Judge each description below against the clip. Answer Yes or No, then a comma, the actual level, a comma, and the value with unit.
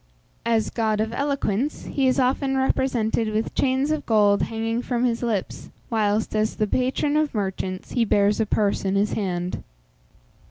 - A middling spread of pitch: Yes, average, 3.8 semitones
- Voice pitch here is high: Yes, high, 225 Hz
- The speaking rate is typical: Yes, average, 165 wpm